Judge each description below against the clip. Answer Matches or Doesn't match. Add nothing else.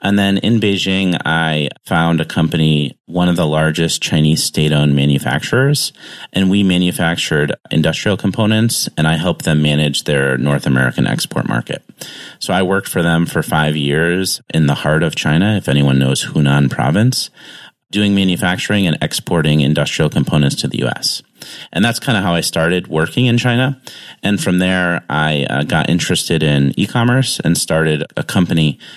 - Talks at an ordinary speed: Matches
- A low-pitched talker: Matches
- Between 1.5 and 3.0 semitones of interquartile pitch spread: Doesn't match